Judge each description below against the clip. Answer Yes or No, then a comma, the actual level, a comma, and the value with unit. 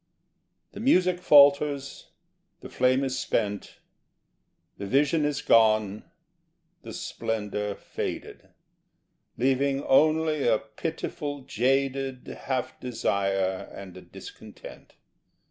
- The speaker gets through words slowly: Yes, slow, 95 wpm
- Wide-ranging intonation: No, average, 4.9 semitones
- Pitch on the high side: No, low, 130 Hz